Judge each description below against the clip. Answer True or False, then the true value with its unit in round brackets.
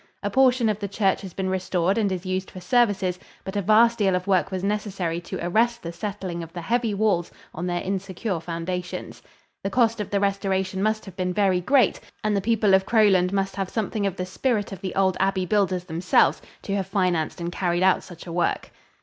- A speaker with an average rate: False (220 wpm)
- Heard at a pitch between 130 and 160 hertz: False (190 Hz)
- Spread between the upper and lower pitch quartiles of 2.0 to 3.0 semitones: True (2.4 semitones)